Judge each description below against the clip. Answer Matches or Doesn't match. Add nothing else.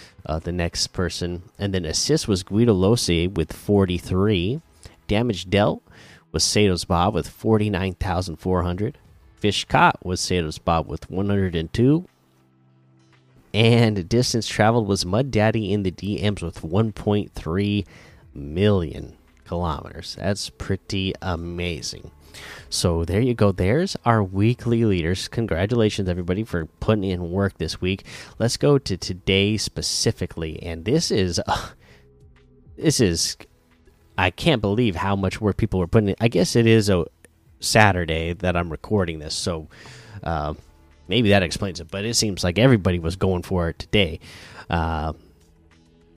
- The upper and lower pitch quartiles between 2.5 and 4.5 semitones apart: Matches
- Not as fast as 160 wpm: Matches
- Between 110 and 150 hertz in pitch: Doesn't match